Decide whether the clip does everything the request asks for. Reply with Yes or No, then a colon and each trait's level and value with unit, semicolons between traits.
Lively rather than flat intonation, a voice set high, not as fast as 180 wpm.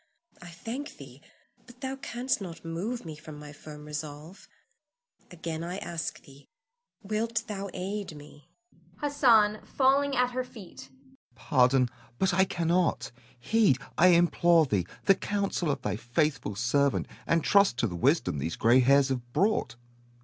No: wide, 6.6 semitones; medium, 170 Hz; average, 150 wpm